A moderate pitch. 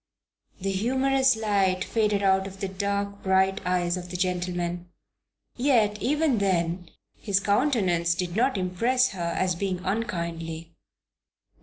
No: high, 195 Hz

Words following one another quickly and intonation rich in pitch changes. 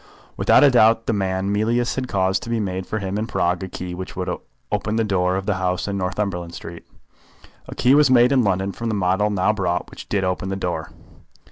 No: fast, 230 wpm; average, 3.0 semitones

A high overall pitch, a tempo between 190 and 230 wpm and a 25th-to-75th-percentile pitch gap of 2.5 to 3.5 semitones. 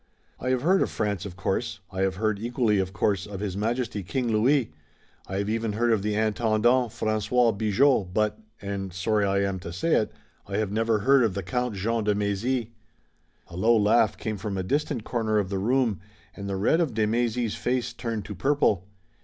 No: low, 110 Hz; fast, 205 wpm; average, 3.2 semitones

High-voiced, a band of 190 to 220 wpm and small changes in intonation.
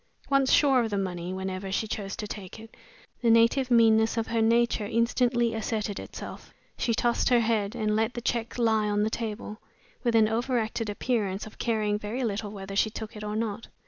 Yes: high, 220 Hz; average, 200 wpm; narrow, 2.0 semitones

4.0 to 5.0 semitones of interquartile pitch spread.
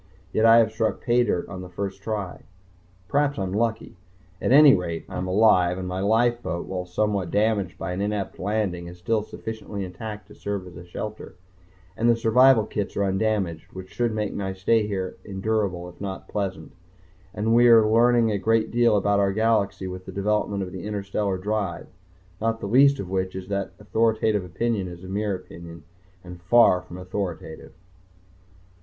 No: average, 3.1 semitones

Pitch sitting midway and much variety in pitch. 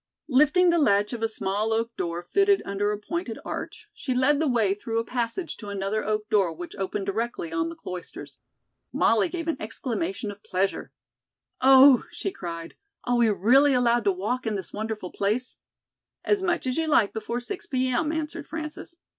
No: high, 230 Hz; wide, 6.0 semitones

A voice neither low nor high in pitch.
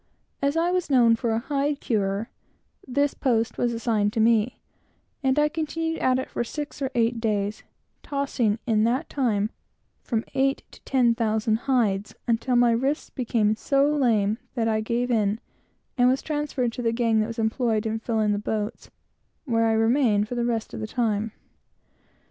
No: high, 235 Hz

